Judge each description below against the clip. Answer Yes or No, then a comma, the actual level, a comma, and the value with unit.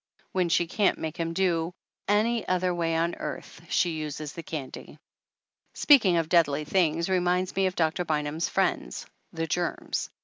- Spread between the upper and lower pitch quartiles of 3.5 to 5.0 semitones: No, narrow, 2.4 semitones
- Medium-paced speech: Yes, average, 160 wpm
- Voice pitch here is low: No, medium, 170 Hz